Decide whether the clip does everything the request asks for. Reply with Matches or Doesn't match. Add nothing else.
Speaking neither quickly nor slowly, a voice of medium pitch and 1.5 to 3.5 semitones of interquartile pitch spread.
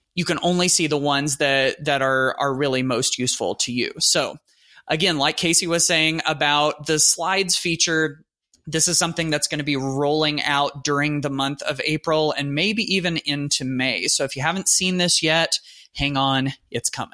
Matches